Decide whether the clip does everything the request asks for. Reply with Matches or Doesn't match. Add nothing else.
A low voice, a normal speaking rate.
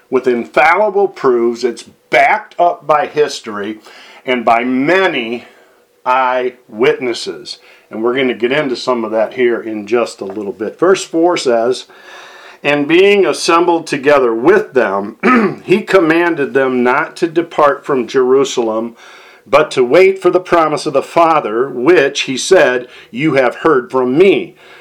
Doesn't match